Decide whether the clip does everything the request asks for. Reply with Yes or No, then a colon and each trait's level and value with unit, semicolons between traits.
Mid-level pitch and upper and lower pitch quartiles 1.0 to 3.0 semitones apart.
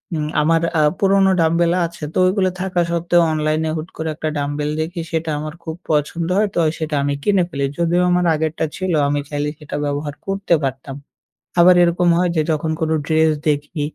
Yes: medium, 160 Hz; narrow, 2.6 semitones